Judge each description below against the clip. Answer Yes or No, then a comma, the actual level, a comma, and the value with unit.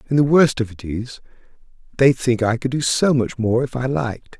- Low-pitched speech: Yes, low, 125 Hz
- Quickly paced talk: Yes, fast, 230 wpm